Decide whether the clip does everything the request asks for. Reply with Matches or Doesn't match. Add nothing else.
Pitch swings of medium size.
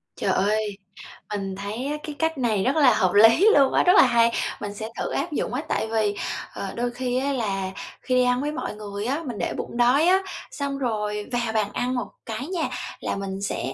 Matches